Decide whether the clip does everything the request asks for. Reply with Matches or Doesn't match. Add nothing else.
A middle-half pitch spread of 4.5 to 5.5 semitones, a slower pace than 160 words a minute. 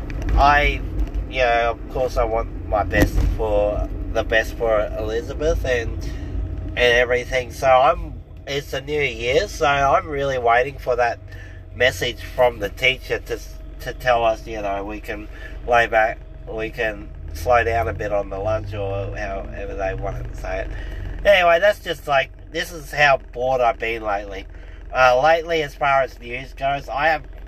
Doesn't match